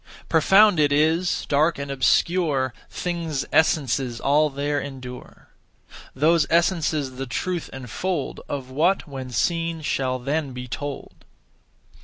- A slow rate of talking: Yes, slow, 120 wpm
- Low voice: No, medium, 145 Hz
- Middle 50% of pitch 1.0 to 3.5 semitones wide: No, average, 3.9 semitones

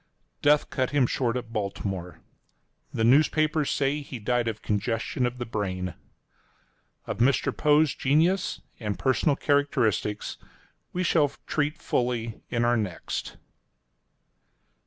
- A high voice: No, low, 125 Hz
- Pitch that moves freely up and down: No, average, 4.6 semitones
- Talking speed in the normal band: No, slow, 120 wpm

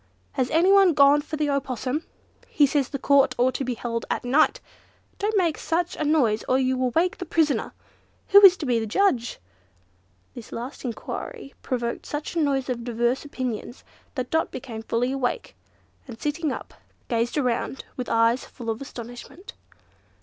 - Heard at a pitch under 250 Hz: No, very high, 265 Hz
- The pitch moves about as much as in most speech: Yes, average, 4.2 semitones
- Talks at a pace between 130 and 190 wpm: Yes, average, 170 wpm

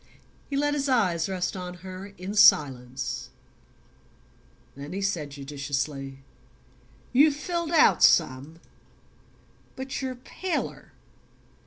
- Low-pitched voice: No, medium, 185 Hz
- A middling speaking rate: No, slow, 105 wpm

